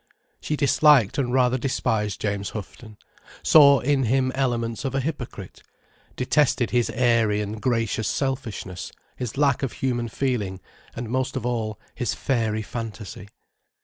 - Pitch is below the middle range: Yes, low, 120 Hz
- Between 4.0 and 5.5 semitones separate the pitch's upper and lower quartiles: No, average, 3.6 semitones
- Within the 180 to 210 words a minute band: No, average, 140 wpm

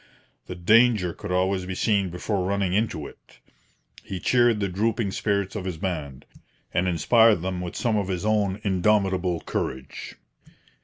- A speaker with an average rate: Yes, average, 155 wpm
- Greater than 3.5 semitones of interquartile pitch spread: No, average, 2.8 semitones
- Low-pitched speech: Yes, very low, 95 Hz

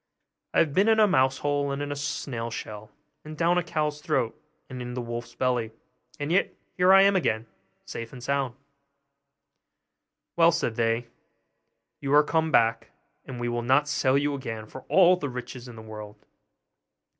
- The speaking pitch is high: No, low, 135 Hz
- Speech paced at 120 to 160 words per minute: No, average, 180 wpm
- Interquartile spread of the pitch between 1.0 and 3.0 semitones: No, average, 4.4 semitones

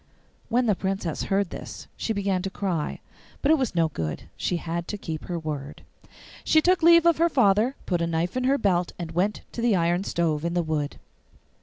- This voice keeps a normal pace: No, fast, 210 wpm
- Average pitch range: No, wide, 5.7 semitones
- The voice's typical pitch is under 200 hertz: Yes, medium, 185 Hz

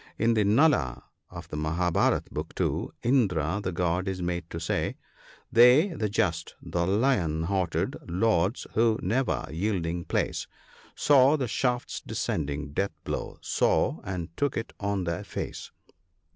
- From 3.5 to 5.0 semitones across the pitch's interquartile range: No, wide, 5.5 semitones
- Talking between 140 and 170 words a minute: Yes, average, 160 wpm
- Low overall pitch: Yes, very low, 95 Hz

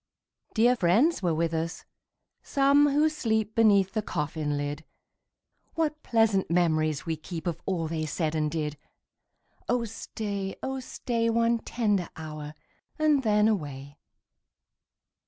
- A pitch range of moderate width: No, wide, 6.7 semitones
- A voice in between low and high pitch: No, high, 195 Hz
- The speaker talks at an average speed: No, slow, 130 wpm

